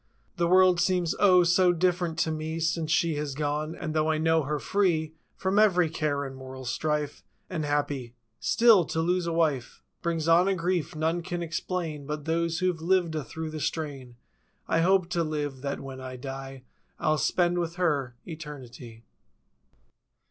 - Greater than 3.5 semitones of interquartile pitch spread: No, average, 3.1 semitones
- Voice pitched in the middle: Yes, medium, 160 Hz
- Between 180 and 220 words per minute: No, average, 170 wpm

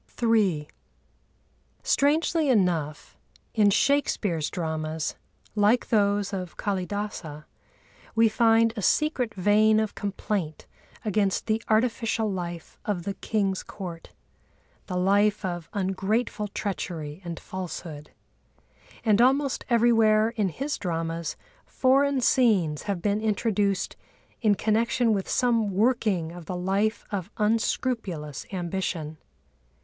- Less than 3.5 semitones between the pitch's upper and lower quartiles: No, average, 4.1 semitones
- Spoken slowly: Yes, slow, 105 wpm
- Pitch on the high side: Yes, high, 205 Hz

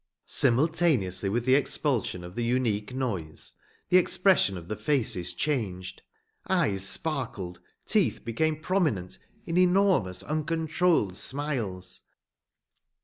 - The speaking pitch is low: Yes, low, 125 Hz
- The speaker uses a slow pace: Yes, slow, 105 wpm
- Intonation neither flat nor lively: No, wide, 8.8 semitones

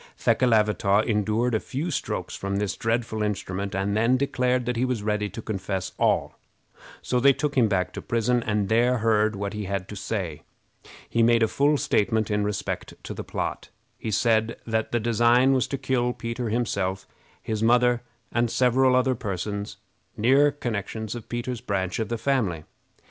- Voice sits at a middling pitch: No, low, 115 Hz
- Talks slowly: No, average, 175 wpm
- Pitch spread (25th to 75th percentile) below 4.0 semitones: Yes, average, 3.1 semitones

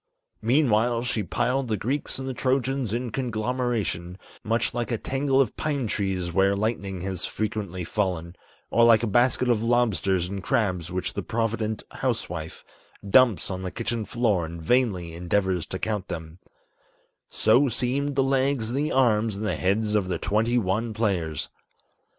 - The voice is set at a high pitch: No, low, 110 Hz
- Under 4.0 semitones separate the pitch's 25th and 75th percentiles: No, average, 4.6 semitones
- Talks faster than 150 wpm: Yes, average, 160 wpm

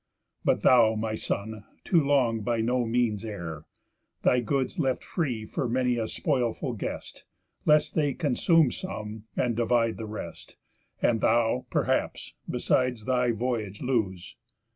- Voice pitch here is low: Yes, low, 120 Hz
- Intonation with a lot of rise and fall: No, average, 2.7 semitones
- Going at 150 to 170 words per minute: No, average, 140 wpm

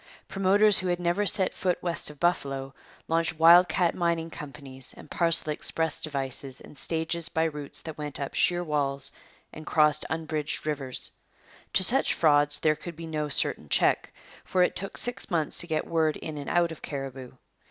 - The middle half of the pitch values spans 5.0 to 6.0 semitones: No, average, 2.9 semitones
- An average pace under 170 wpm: No, average, 180 wpm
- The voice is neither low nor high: Yes, medium, 160 Hz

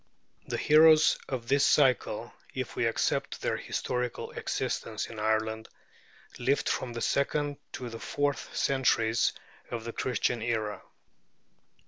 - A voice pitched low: Yes, low, 125 Hz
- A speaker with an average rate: No, slow, 125 wpm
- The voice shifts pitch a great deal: No, average, 3.7 semitones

